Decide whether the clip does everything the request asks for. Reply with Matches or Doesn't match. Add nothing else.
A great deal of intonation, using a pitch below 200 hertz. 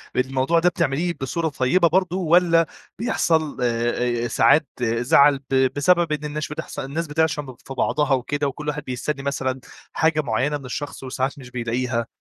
Doesn't match